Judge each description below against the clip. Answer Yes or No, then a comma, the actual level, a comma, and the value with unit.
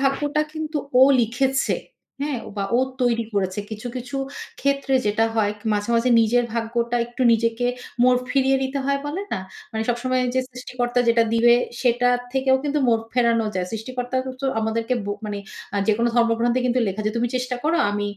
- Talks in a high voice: Yes, high, 245 Hz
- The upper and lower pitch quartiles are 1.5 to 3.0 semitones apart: Yes, narrow, 2.5 semitones